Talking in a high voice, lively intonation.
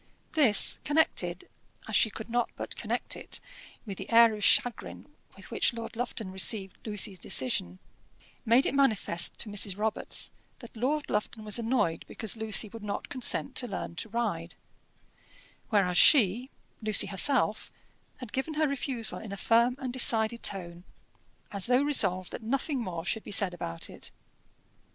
No: high, 220 Hz; average, 3.9 semitones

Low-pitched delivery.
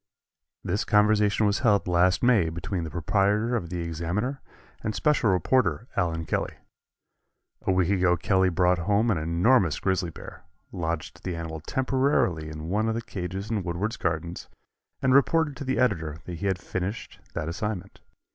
Yes: very low, 95 Hz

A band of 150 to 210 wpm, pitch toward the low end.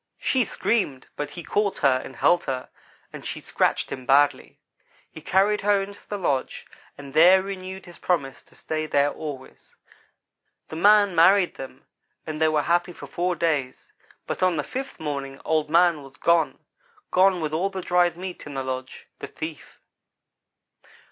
No: average, 170 wpm; medium, 165 Hz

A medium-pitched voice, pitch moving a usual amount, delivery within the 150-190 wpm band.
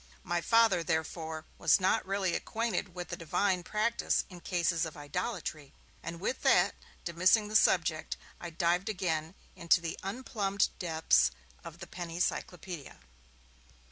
No: medium, 175 Hz; average, 3.1 semitones; average, 140 wpm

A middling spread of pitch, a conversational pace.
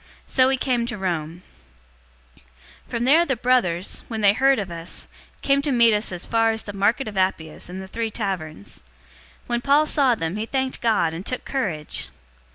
No: wide, 5.7 semitones; average, 190 wpm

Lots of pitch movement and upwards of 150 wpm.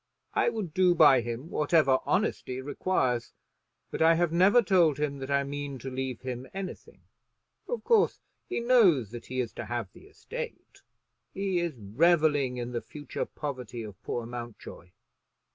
Yes: wide, 5.9 semitones; average, 160 wpm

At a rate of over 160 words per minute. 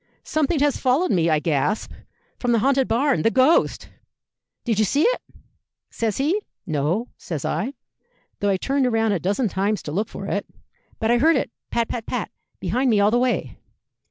Yes: average, 185 wpm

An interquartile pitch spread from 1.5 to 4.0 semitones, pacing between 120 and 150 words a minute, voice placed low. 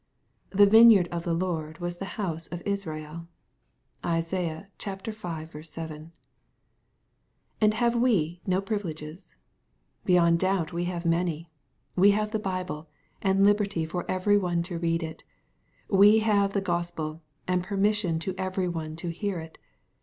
No: average, 3.2 semitones; average, 145 wpm; medium, 180 Hz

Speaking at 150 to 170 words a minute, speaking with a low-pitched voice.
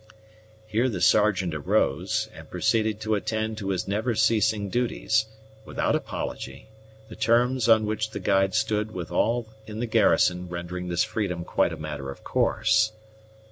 Yes: average, 155 wpm; low, 110 Hz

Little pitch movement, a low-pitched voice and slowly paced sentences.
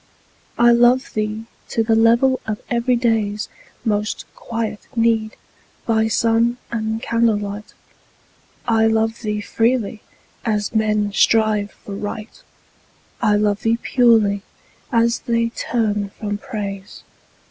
No: narrow, 1.7 semitones; high, 220 Hz; slow, 115 wpm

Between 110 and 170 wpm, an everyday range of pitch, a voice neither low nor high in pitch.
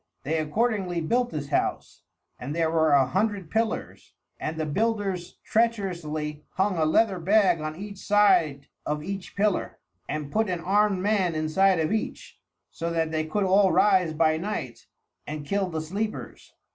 Yes: average, 160 wpm; average, 4.7 semitones; medium, 180 Hz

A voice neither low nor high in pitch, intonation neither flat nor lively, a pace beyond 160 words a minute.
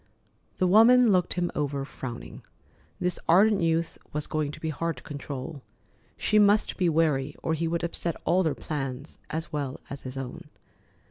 Yes: medium, 160 Hz; average, 3.9 semitones; average, 175 wpm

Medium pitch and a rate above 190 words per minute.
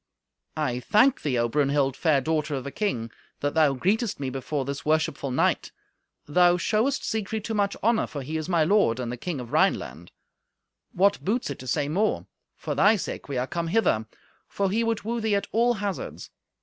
Yes: medium, 160 Hz; average, 200 wpm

